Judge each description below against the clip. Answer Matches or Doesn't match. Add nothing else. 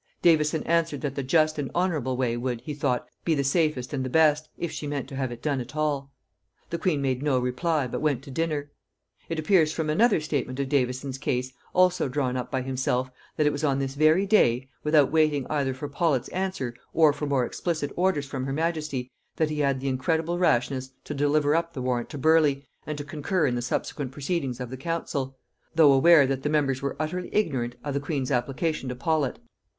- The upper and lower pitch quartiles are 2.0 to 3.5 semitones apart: Matches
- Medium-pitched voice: Matches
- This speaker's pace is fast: Matches